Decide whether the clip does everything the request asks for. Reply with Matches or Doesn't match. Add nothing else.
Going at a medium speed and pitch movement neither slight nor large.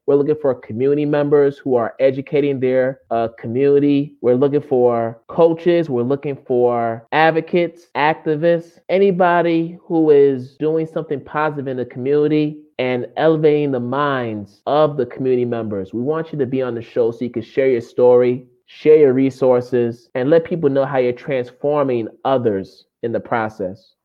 Matches